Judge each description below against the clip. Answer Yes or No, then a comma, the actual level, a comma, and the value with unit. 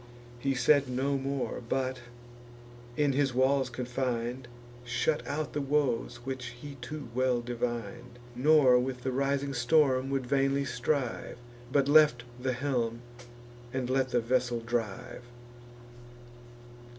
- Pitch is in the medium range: No, low, 130 Hz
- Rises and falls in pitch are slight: Yes, narrow, 2.2 semitones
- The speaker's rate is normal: No, slow, 125 wpm